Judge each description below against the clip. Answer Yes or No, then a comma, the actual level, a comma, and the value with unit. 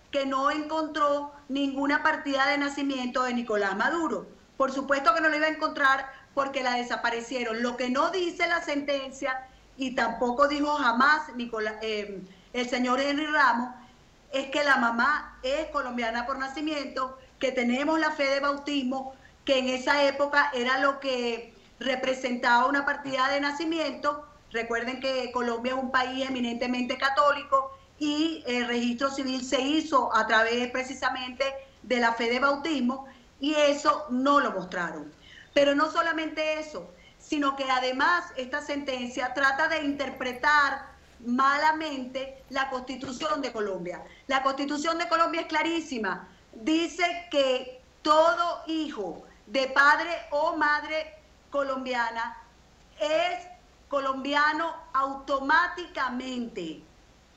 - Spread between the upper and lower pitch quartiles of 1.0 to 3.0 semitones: Yes, average, 2.7 semitones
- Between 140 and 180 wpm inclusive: No, average, 130 wpm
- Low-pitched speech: No, very high, 270 Hz